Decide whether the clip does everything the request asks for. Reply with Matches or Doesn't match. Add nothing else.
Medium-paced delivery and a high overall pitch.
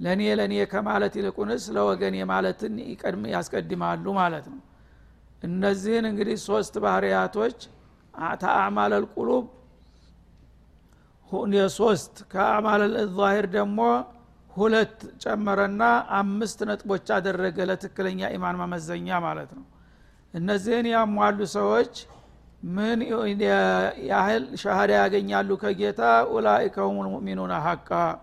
Matches